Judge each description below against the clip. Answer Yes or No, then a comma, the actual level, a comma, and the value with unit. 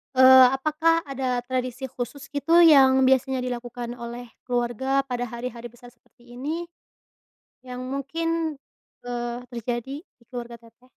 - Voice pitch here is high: Yes, very high, 255 Hz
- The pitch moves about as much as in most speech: No, narrow, 2.1 semitones